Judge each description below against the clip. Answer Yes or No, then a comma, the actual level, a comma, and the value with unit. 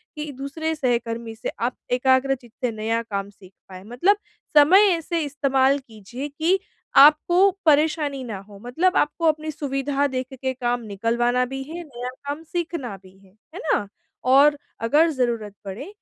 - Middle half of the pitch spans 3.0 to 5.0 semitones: Yes, average, 4.4 semitones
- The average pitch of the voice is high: Yes, very high, 270 Hz